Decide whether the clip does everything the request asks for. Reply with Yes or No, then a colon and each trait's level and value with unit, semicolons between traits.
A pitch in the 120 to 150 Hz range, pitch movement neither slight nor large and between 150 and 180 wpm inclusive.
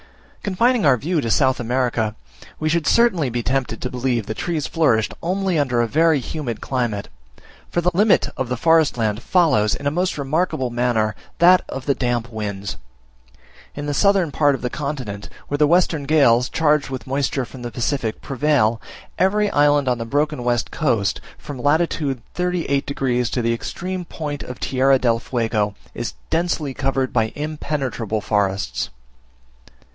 Yes: low, 135 Hz; average, 4.7 semitones; average, 165 wpm